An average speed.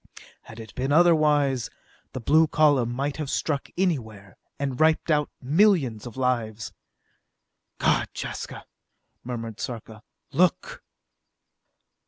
No: slow, 110 wpm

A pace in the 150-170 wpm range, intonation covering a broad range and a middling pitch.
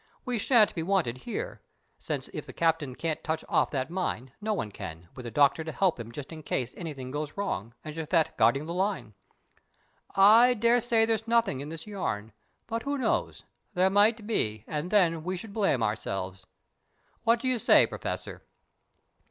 No: average, 180 wpm; wide, 8.2 semitones; medium, 165 Hz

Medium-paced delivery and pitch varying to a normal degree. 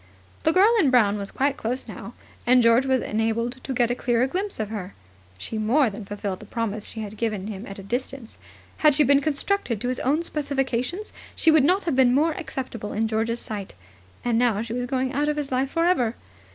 No: fast, 220 wpm; average, 4.2 semitones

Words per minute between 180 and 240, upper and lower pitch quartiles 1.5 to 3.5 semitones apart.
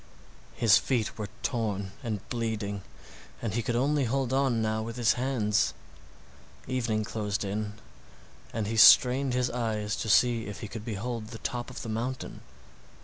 No: average, 160 wpm; average, 2.7 semitones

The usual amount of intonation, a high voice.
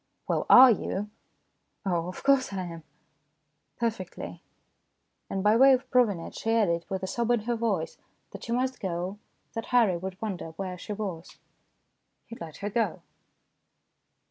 Yes: average, 4.3 semitones; high, 205 Hz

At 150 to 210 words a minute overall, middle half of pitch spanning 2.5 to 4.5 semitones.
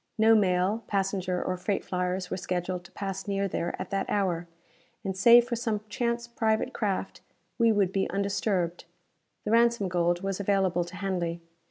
Yes: average, 170 wpm; average, 2.8 semitones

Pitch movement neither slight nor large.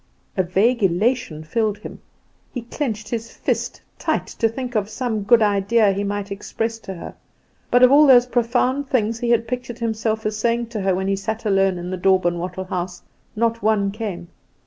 Yes: average, 3.4 semitones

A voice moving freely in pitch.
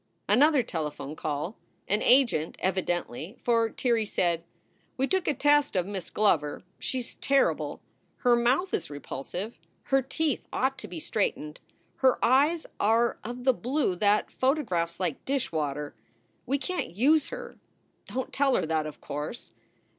Yes: wide, 8.0 semitones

